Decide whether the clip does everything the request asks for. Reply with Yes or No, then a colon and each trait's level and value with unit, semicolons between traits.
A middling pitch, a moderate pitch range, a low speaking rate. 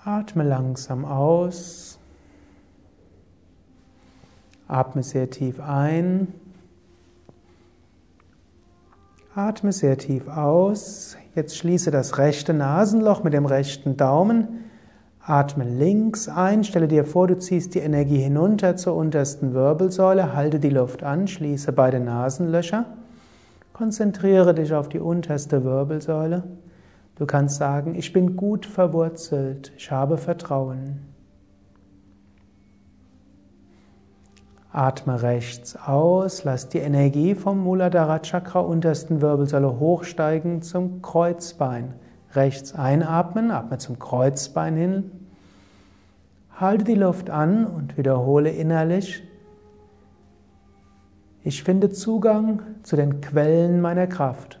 No: medium, 145 Hz; wide, 6.5 semitones; slow, 100 wpm